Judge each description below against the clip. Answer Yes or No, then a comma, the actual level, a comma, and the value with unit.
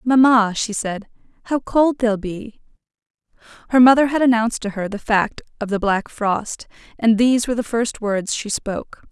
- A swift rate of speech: No, average, 180 wpm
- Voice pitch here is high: Yes, high, 225 Hz